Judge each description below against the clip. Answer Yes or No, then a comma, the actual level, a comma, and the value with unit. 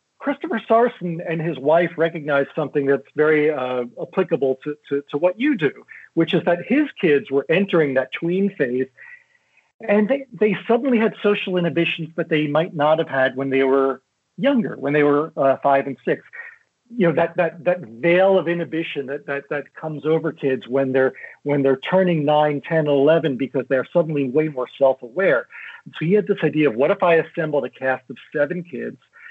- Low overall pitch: No, medium, 160 Hz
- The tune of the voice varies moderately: Yes, average, 4.4 semitones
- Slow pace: No, average, 195 wpm